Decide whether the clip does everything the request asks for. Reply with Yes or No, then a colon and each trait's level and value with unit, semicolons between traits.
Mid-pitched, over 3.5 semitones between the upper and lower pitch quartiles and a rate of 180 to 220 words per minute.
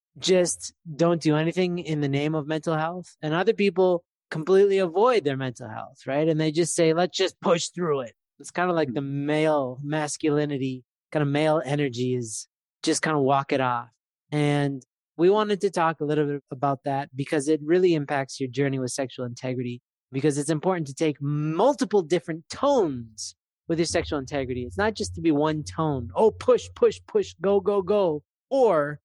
Yes: medium, 155 Hz; average, 4.0 semitones; average, 190 wpm